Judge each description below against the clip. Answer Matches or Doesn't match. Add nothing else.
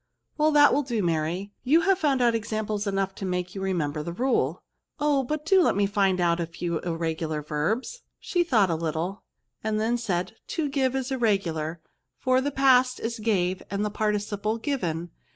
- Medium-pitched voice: Doesn't match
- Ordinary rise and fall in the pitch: Doesn't match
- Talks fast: Matches